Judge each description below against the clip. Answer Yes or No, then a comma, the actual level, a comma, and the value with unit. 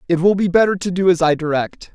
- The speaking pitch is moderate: Yes, medium, 180 Hz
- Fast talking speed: Yes, fast, 275 wpm